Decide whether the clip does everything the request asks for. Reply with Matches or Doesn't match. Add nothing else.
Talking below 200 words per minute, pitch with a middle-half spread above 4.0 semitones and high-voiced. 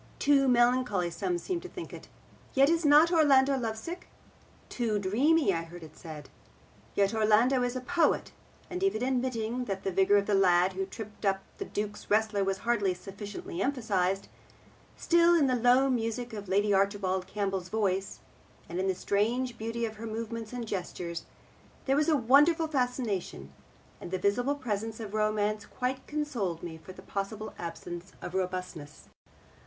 Matches